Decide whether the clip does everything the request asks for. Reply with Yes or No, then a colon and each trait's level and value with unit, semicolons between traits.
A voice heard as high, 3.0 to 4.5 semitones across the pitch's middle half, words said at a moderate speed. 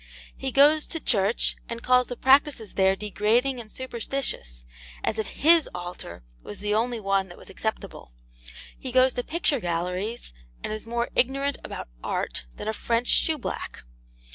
No: high, 235 Hz; average, 5.0 semitones; average, 160 wpm